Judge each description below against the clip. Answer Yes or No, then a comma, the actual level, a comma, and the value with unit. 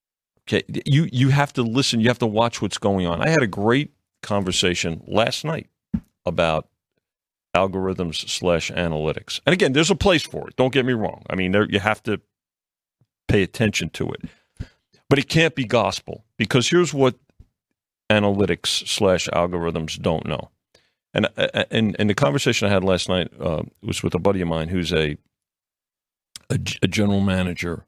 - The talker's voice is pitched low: Yes, low, 100 Hz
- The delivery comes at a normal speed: Yes, average, 175 wpm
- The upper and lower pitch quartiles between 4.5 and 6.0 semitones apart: Yes, average, 5.1 semitones